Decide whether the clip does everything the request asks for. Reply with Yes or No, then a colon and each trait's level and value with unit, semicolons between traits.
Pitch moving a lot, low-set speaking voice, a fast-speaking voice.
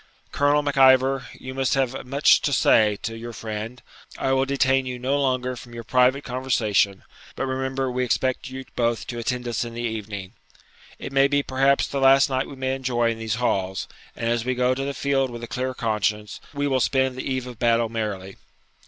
No: narrow, 2.4 semitones; low, 130 Hz; fast, 210 wpm